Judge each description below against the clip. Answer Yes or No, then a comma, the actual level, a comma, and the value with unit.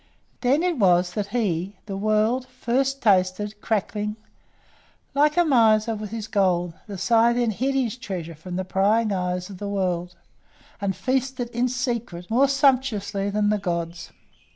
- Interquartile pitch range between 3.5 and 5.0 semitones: Yes, average, 4.5 semitones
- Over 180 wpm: No, average, 155 wpm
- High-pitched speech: Yes, high, 210 Hz